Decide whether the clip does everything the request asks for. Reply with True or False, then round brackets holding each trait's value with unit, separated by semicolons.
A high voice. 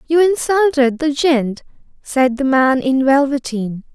True (275 Hz)